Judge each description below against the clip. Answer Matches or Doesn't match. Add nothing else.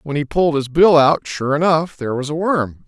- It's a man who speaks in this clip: Matches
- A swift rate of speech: Matches